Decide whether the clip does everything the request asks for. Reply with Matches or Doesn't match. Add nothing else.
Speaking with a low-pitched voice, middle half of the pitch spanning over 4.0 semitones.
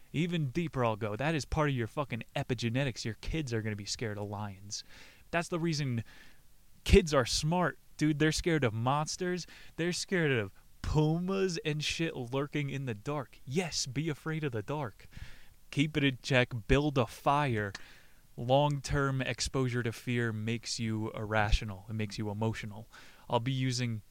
Matches